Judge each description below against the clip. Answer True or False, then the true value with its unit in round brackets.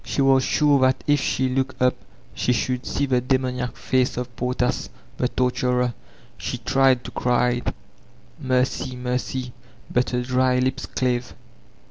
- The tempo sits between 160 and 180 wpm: False (145 wpm)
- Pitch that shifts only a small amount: True (0.9 semitones)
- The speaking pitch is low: True (125 Hz)